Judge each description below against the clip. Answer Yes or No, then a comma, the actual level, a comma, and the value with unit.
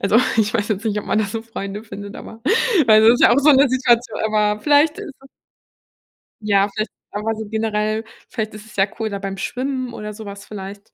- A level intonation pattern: Yes, narrow, 2.1 semitones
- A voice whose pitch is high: Yes, high, 215 Hz